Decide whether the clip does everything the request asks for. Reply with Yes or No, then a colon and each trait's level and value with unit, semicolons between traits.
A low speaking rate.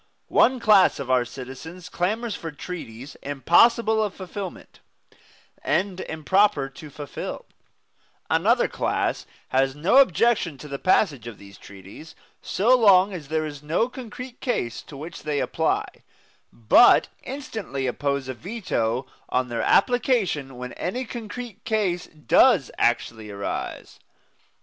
Yes: slow, 130 wpm